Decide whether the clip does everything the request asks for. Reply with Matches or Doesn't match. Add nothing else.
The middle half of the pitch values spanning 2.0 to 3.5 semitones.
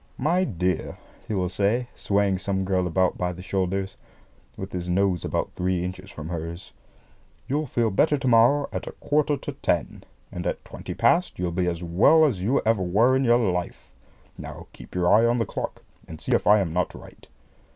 Doesn't match